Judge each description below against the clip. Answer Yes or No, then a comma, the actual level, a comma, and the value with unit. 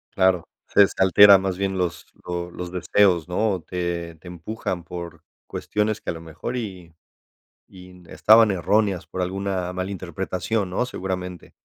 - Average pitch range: No, narrow, 2.1 semitones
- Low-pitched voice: Yes, very low, 90 Hz